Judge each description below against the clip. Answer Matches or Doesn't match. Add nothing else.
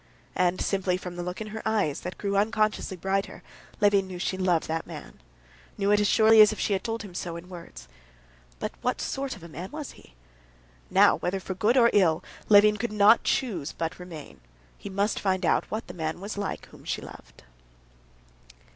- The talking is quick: Matches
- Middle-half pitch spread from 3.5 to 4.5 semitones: Doesn't match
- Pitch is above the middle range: Matches